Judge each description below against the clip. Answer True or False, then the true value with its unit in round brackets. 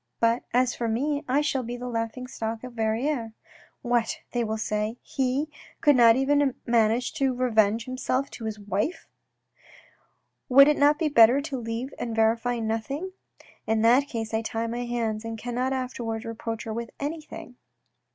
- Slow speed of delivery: False (180 wpm)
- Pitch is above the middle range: True (240 Hz)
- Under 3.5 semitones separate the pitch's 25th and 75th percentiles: True (2.8 semitones)